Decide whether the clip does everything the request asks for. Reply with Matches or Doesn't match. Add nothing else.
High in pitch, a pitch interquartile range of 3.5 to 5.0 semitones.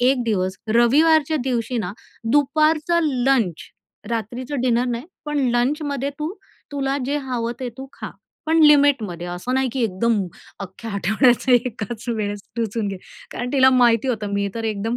Matches